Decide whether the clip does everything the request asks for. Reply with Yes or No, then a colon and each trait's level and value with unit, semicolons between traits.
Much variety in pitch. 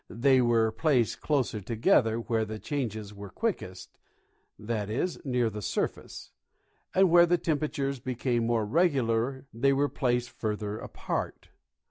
No: average, 4.0 semitones